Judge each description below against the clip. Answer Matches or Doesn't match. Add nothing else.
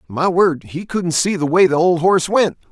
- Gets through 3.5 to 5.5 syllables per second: Matches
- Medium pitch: Matches